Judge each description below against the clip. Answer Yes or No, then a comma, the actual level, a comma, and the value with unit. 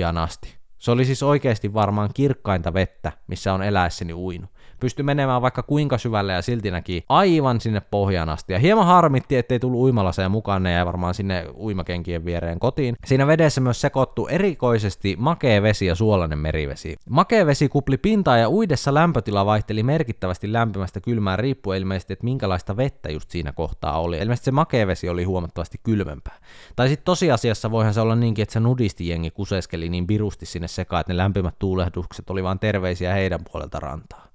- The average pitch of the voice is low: Yes, low, 105 Hz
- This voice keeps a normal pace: No, fast, 175 wpm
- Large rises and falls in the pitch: Yes, wide, 5.9 semitones